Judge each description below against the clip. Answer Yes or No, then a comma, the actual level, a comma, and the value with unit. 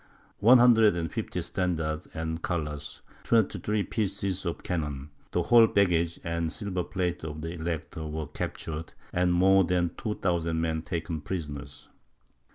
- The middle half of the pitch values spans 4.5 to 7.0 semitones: No, average, 3.2 semitones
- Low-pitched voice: Yes, very low, 85 Hz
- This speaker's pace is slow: No, average, 145 wpm